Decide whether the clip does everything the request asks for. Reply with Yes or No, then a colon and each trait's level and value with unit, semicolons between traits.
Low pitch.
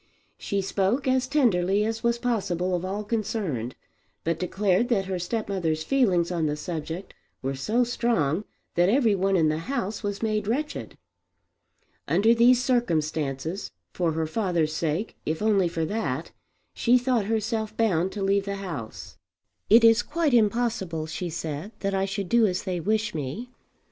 No: high, 195 Hz